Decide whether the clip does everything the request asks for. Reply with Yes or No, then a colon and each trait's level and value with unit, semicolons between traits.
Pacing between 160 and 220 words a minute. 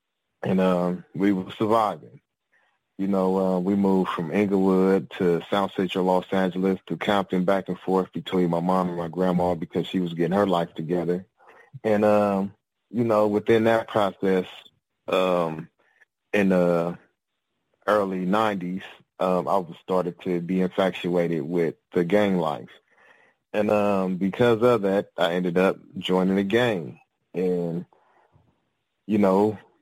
No: average, 145 wpm